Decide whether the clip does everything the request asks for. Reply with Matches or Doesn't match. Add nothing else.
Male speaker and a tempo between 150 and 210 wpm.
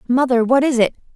Doesn't match